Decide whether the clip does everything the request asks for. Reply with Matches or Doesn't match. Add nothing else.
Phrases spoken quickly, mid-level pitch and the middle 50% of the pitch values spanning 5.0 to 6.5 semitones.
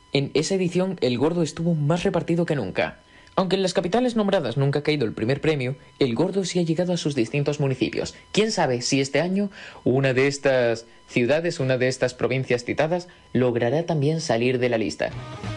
Matches